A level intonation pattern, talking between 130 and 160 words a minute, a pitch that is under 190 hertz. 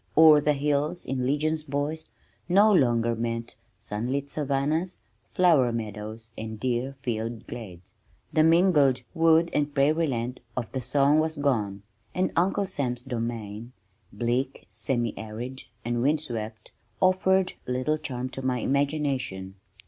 No: average, 4.7 semitones; slow, 135 wpm; low, 135 Hz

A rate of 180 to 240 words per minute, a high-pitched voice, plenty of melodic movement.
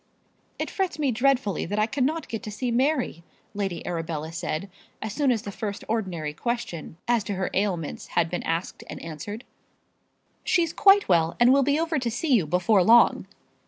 Yes: average, 185 wpm; high, 215 Hz; wide, 6.8 semitones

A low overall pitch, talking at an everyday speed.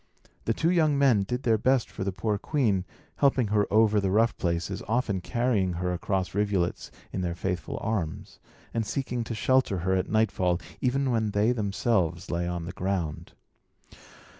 Yes: low, 105 Hz; average, 170 wpm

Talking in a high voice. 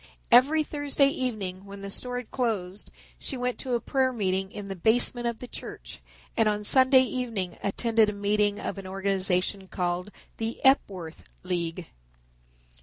Yes: high, 210 Hz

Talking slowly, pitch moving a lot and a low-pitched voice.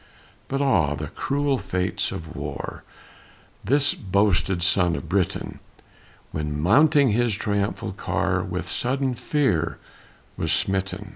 Yes: slow, 120 wpm; wide, 8.0 semitones; low, 100 Hz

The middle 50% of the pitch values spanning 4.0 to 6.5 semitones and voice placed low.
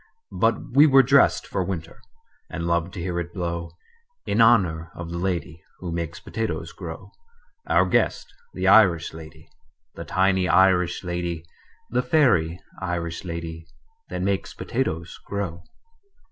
No: narrow, 2.5 semitones; very low, 85 Hz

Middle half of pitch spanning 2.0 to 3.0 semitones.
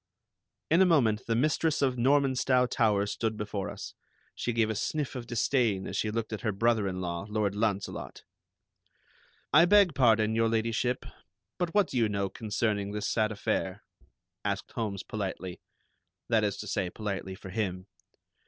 No: average, 3.5 semitones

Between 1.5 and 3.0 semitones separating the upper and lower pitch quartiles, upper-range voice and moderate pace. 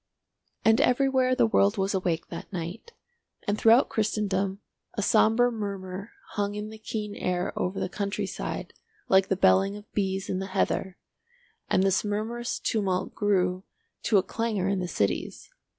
Yes: narrow, 2.5 semitones; high, 200 Hz; average, 160 wpm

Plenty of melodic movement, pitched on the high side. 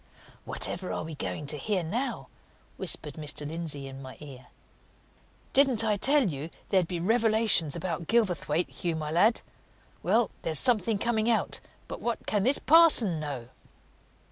No: wide, 6.7 semitones; medium, 180 Hz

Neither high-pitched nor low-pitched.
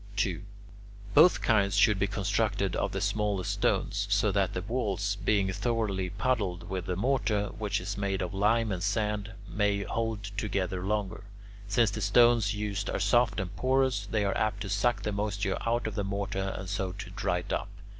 No: low, 100 Hz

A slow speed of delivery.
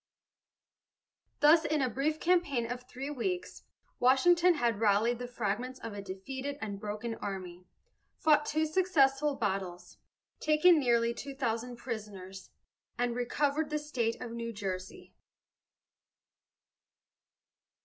Yes: slow, 120 wpm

